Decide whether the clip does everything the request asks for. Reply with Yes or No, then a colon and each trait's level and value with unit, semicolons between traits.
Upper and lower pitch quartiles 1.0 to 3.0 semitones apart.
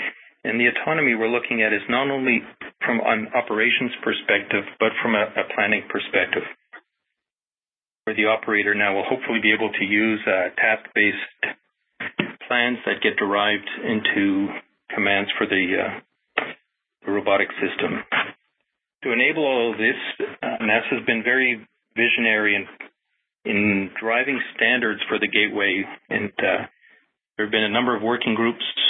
Yes: average, 2.7 semitones